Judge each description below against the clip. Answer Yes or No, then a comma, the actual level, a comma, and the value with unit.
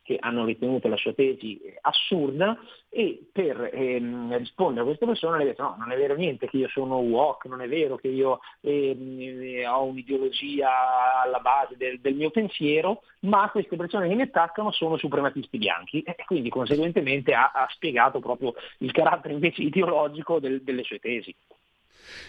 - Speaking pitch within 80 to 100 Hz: No, medium, 140 Hz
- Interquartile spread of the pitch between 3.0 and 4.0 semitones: No, wide, 5.6 semitones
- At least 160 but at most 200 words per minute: Yes, fast, 170 wpm